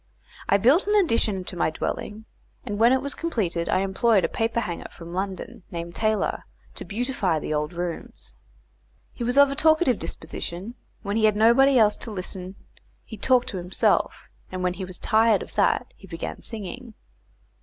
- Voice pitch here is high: Yes, high, 210 Hz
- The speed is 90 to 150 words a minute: No, average, 175 wpm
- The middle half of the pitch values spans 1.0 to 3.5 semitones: No, average, 4.8 semitones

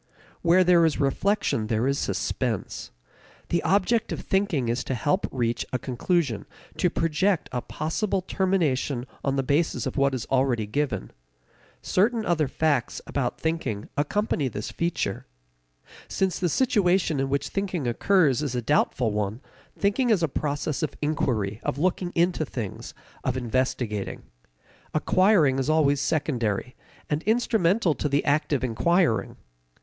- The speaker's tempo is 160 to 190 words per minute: No, average, 145 wpm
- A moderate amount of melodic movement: No, wide, 5.7 semitones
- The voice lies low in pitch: No, medium, 150 Hz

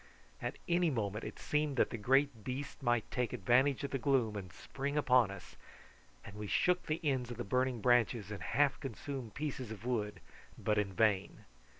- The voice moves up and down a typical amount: Yes, average, 4.6 semitones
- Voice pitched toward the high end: No, low, 125 Hz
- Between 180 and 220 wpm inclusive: Yes, average, 190 wpm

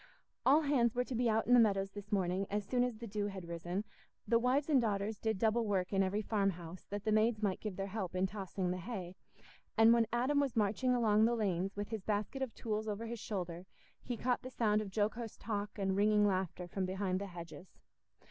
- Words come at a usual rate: No, fast, 225 wpm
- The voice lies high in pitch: Yes, high, 210 Hz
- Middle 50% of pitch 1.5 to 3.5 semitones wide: Yes, average, 3.2 semitones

